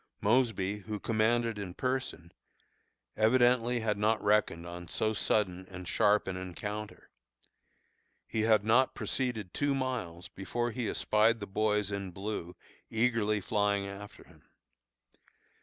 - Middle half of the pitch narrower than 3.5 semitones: Yes, average, 2.8 semitones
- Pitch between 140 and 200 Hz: No, low, 105 Hz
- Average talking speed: No, slow, 125 wpm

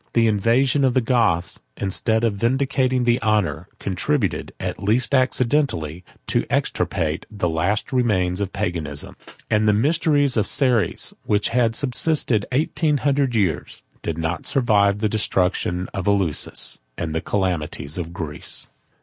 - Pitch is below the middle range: Yes, low, 105 Hz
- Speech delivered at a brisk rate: No, average, 140 wpm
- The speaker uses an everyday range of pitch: No, wide, 6.0 semitones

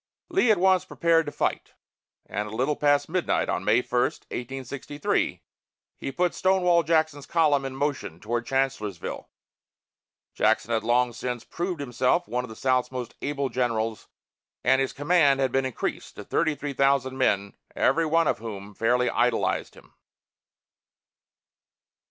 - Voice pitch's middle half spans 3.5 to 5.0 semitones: Yes, average, 4.4 semitones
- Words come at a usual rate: Yes, average, 150 wpm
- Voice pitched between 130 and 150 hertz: Yes, low, 135 Hz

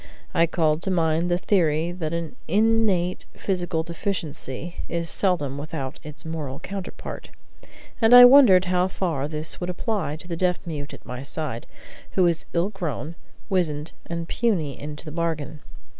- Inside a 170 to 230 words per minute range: No, average, 160 wpm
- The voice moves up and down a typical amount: Yes, average, 3.1 semitones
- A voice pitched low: No, medium, 170 Hz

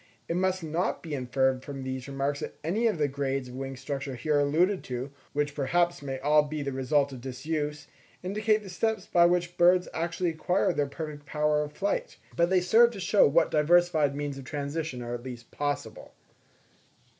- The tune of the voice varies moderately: Yes, average, 4.1 semitones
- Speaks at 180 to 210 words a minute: Yes, average, 190 wpm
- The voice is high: No, medium, 150 Hz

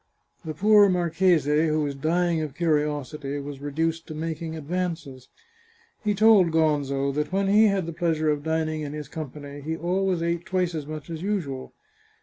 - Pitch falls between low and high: Yes, medium, 160 Hz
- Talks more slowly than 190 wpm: Yes, average, 170 wpm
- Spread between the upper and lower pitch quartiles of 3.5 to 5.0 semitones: No, average, 3.0 semitones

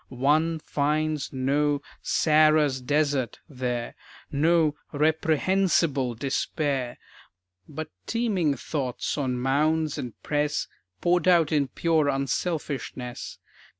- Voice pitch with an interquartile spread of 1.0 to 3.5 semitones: Yes, average, 2.8 semitones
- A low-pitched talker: No, medium, 150 Hz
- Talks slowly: Yes, slow, 90 wpm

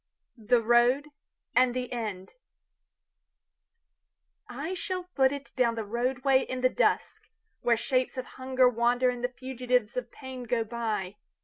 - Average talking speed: No, slow, 125 wpm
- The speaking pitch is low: No, very high, 250 Hz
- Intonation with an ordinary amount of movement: No, narrow, 1.7 semitones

